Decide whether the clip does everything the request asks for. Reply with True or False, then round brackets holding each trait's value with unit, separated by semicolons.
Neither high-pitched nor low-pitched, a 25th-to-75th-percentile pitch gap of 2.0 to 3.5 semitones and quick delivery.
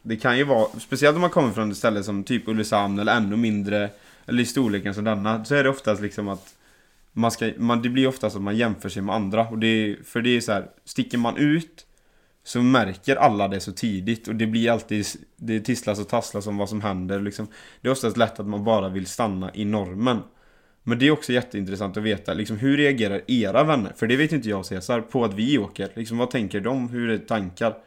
False (110 Hz; 2.9 semitones; 240 wpm)